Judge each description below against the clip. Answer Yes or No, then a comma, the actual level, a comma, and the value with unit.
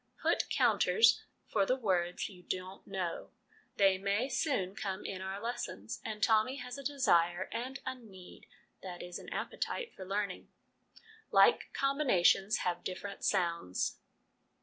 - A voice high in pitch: Yes, high, 195 Hz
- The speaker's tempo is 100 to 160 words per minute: Yes, average, 145 wpm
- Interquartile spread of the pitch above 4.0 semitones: Yes, average, 5.1 semitones